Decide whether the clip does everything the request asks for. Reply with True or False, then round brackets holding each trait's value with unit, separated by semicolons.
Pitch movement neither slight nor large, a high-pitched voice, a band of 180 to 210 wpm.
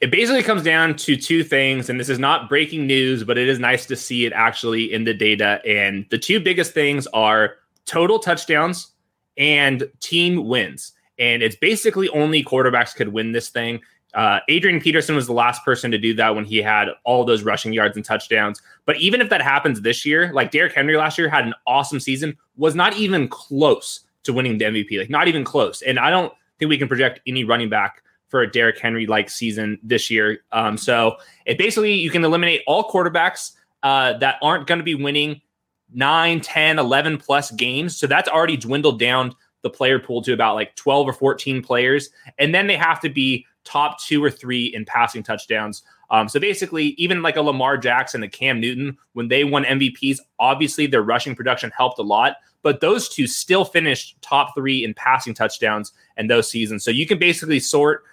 False (4.8 semitones; 135 Hz; 205 wpm)